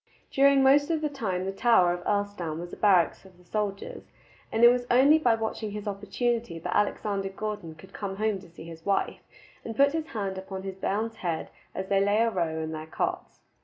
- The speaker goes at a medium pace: No, fast, 215 wpm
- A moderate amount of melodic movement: Yes, average, 4.0 semitones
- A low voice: No, high, 200 Hz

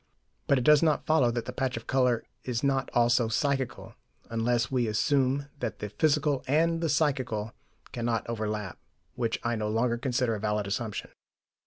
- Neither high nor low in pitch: No, low, 120 Hz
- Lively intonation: No, average, 3.4 semitones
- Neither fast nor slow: Yes, average, 170 wpm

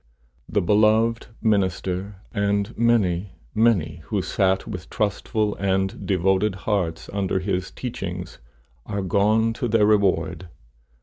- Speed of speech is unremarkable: No, slow, 115 wpm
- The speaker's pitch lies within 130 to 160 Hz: No, low, 100 Hz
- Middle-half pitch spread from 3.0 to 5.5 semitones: No, narrow, 2.4 semitones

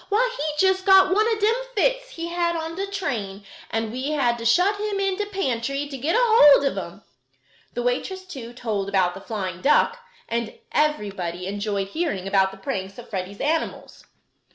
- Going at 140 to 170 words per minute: No, average, 185 wpm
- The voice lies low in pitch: No, very high, 280 Hz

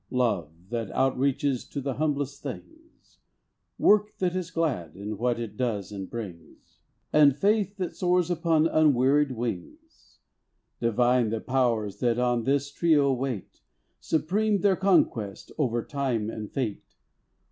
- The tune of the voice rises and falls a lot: Yes, wide, 5.7 semitones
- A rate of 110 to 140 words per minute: Yes, slow, 135 wpm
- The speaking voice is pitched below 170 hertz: Yes, low, 135 Hz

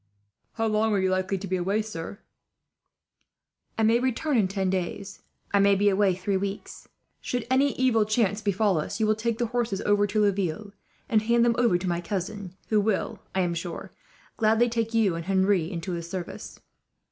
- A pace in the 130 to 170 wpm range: No, average, 195 wpm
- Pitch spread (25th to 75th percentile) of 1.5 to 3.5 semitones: Yes, average, 2.9 semitones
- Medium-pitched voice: No, high, 205 Hz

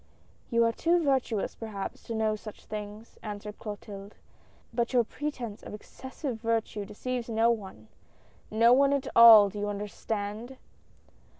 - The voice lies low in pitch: No, high, 220 Hz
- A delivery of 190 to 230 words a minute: No, average, 160 wpm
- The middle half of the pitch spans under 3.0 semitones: Yes, narrow, 2.4 semitones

